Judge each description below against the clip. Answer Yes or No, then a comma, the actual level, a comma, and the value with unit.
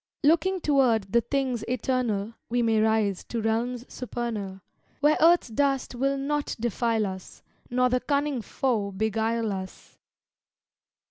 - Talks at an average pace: No, slow, 130 wpm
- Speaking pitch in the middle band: No, high, 240 Hz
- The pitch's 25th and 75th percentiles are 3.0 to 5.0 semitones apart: Yes, average, 3.7 semitones